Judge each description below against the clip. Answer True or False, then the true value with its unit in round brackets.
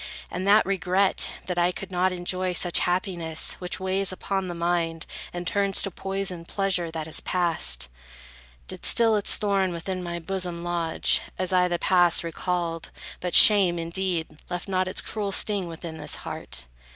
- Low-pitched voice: False (180 Hz)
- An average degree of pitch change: False (2.1 semitones)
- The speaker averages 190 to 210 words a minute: False (165 wpm)